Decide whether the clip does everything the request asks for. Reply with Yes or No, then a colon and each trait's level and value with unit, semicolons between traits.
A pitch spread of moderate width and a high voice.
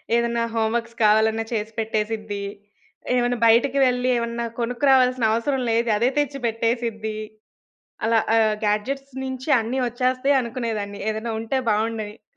No: narrow, 2.3 semitones; high, 230 Hz